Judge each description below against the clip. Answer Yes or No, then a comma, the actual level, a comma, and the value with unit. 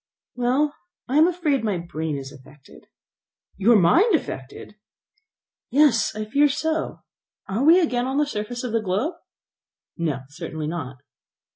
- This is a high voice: Yes, high, 230 Hz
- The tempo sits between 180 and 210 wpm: No, average, 140 wpm